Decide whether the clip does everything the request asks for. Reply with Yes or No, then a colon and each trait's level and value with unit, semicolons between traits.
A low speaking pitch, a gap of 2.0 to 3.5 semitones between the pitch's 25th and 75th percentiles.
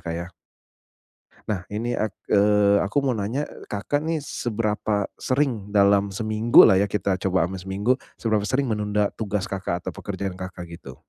Yes: low, 105 Hz; narrow, 2.6 semitones